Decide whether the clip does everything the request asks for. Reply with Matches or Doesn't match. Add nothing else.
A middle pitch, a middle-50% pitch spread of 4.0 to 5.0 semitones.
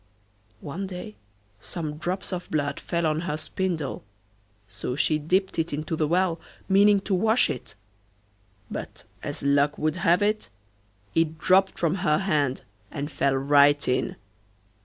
Matches